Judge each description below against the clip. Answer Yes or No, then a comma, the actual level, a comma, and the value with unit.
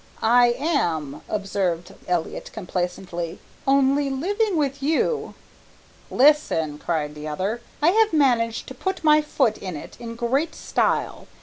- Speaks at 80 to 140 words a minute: Yes, slow, 135 wpm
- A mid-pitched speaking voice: No, high, 240 Hz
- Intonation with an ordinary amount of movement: No, wide, 8.7 semitones